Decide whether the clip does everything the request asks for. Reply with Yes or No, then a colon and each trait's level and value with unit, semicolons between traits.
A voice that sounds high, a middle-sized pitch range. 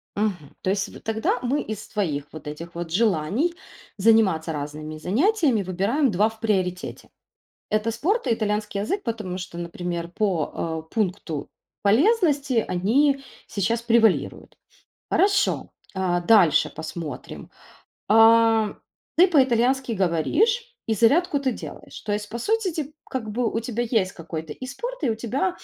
No: high, 220 Hz; wide, 6.4 semitones